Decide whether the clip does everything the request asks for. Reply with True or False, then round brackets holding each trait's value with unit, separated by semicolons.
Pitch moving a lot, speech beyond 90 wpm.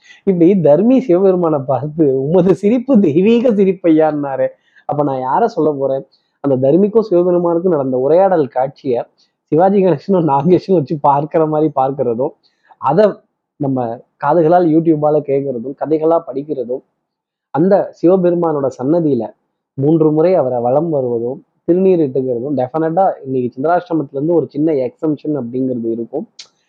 False (4.6 semitones; 115 wpm)